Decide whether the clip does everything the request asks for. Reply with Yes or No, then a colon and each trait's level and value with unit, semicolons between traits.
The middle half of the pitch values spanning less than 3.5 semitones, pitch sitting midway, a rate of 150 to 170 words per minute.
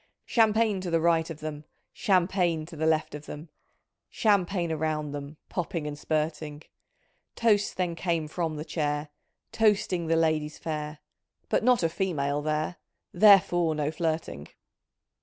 No: average, 2.9 semitones; medium, 160 Hz; average, 140 wpm